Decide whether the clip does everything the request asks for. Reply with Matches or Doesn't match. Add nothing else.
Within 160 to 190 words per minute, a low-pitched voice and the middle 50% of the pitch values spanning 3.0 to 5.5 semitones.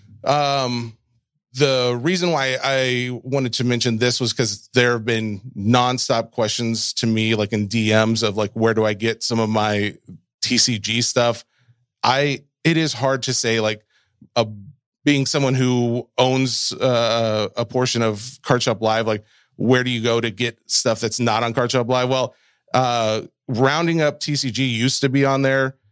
Doesn't match